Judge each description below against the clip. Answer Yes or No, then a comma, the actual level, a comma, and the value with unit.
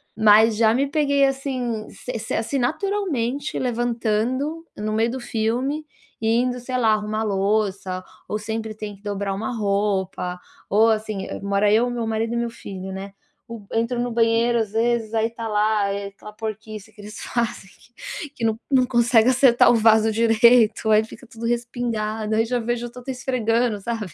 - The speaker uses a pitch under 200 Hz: No, high, 225 Hz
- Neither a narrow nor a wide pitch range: No, narrow, 2.2 semitones